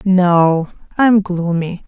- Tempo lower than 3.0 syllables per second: Yes, 2.7 syllables/s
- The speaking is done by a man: No, female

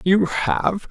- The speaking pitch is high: Yes, high, 195 Hz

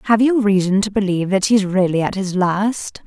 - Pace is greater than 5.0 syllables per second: Yes, 5.2 syllables/s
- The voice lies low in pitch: No, high, 200 Hz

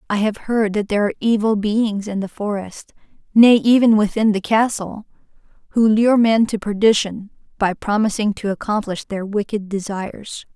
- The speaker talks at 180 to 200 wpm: No, average, 150 wpm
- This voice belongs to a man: No, female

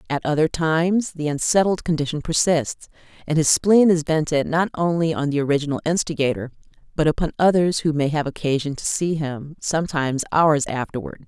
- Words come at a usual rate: Yes, average, 165 wpm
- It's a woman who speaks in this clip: Yes, female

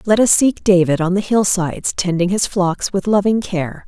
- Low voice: No, high, 190 Hz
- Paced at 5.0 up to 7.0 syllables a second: No, 4.8 syllables/s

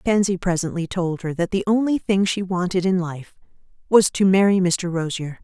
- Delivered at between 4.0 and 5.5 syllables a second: Yes, 5.1 syllables/s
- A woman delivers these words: Yes, female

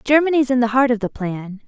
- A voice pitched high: Yes, high, 240 Hz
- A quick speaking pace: Yes, fast, 250 wpm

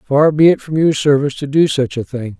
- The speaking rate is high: Yes, fast, 275 wpm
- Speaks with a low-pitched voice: No, medium, 145 Hz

